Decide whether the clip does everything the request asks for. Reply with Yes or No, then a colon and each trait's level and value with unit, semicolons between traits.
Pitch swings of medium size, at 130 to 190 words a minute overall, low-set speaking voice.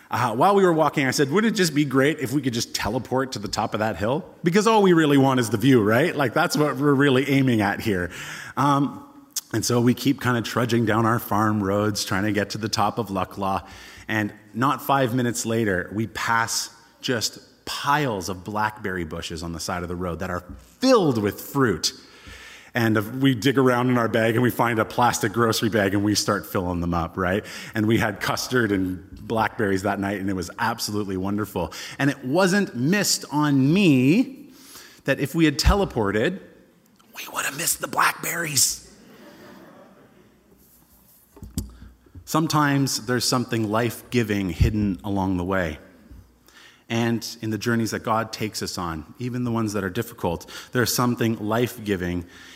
Yes: average, 5.0 semitones; average, 185 wpm; low, 115 Hz